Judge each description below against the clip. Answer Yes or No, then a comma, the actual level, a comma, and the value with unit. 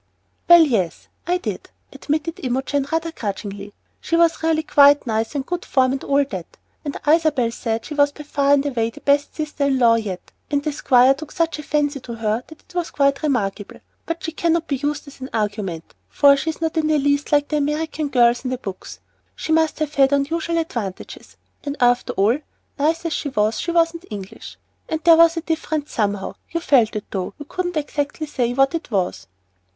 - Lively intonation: No, average, 4.8 semitones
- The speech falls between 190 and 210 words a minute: Yes, average, 200 wpm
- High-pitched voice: Yes, very high, 285 Hz